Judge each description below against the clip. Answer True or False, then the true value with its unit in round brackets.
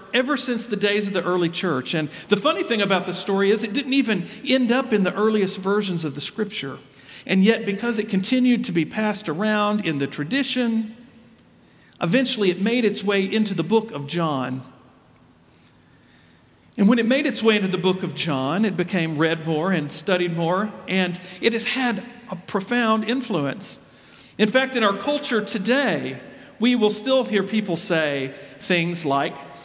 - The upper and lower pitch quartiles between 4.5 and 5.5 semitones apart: True (4.8 semitones)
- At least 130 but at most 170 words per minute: False (180 wpm)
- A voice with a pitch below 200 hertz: False (205 Hz)